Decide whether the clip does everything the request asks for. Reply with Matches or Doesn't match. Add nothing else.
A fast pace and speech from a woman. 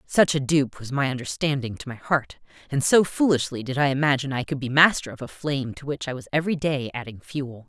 Matches